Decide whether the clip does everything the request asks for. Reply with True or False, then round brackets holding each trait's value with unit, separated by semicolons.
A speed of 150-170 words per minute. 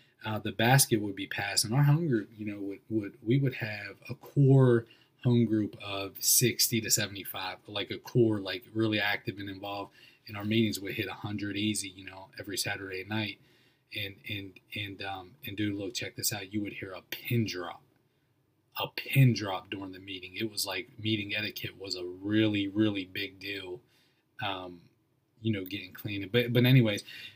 False (195 wpm)